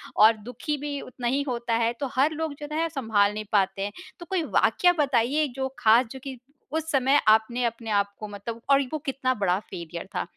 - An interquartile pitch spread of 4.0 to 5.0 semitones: Yes, average, 4.6 semitones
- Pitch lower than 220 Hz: No, high, 245 Hz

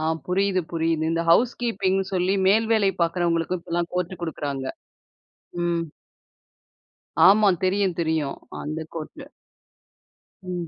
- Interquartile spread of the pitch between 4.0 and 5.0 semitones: No, average, 2.7 semitones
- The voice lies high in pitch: No, medium, 180 Hz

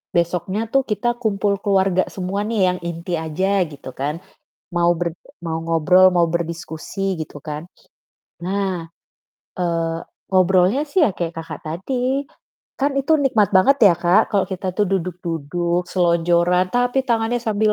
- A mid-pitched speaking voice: Yes, medium, 180 Hz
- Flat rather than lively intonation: No, average, 3.3 semitones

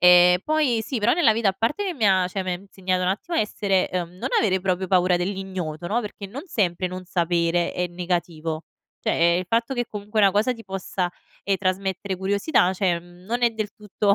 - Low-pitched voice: No, high, 190 Hz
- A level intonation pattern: No, average, 3.1 semitones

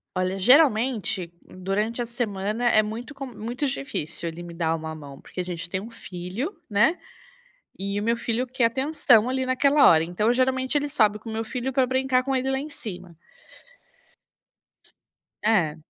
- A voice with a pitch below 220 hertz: No, high, 225 Hz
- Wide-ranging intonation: Yes, wide, 5.9 semitones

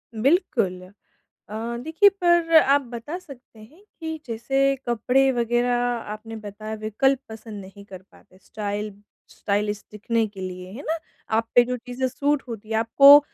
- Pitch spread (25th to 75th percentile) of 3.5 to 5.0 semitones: Yes, average, 4.4 semitones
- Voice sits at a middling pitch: No, high, 235 Hz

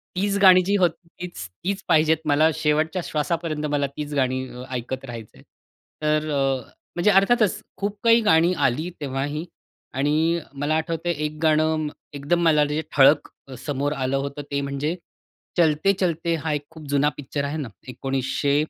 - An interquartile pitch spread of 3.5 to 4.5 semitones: No, average, 3.1 semitones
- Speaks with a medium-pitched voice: Yes, medium, 150 Hz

